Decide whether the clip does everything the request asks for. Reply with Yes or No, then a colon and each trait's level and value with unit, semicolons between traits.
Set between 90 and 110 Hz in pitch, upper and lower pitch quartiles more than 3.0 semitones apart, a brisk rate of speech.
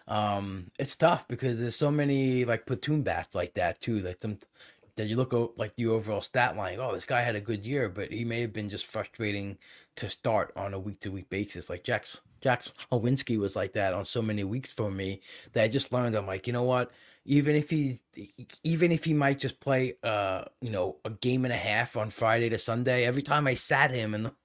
No: low, 120 Hz; average, 3.5 semitones; fast, 230 wpm